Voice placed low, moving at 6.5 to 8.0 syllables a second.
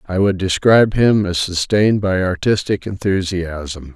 No: very low, 95 Hz; 4.4 syllables/s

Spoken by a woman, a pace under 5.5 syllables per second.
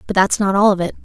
No: female; 7.2 syllables/s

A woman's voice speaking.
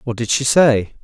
No: male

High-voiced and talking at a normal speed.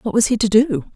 No: high, 220 Hz; fast, 315 wpm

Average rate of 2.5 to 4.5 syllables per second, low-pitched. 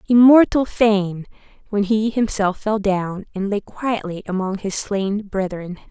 No: 4.0 syllables/s; high, 205 Hz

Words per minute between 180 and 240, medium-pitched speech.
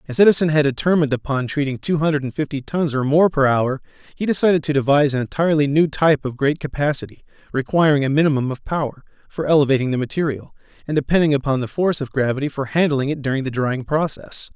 Yes: average, 200 wpm; medium, 145 Hz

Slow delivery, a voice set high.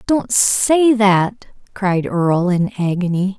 Yes: slow, 125 wpm; high, 200 Hz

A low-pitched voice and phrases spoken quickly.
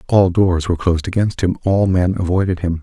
Yes: very low, 90 Hz; fast, 215 wpm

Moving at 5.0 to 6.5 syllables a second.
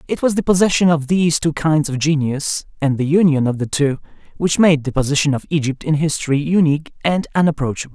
Yes: 6.0 syllables/s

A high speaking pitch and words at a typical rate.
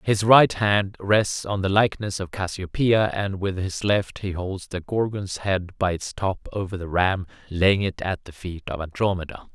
No: very low, 95 Hz; average, 195 wpm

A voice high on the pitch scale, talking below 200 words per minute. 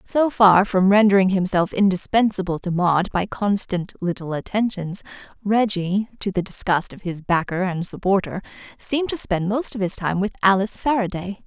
Yes: high, 195 Hz; average, 160 wpm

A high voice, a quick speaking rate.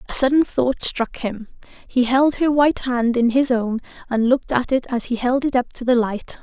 Yes: very high, 250 Hz; fast, 235 wpm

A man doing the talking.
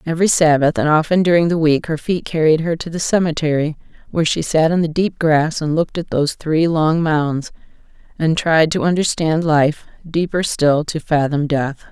No: female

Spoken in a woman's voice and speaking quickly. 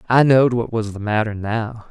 No: male; fast, 220 wpm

